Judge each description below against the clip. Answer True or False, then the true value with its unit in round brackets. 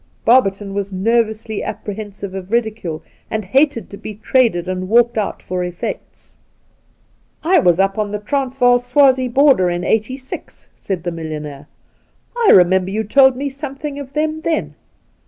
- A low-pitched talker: False (220 Hz)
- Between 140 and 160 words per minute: True (155 wpm)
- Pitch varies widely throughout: True (5.8 semitones)